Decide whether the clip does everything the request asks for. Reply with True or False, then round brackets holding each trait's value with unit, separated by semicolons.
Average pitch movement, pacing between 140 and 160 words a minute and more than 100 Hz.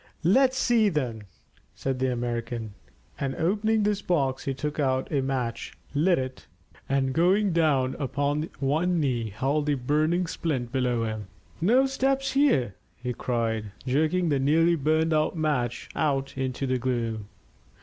True (4.9 semitones; 150 wpm; 140 Hz)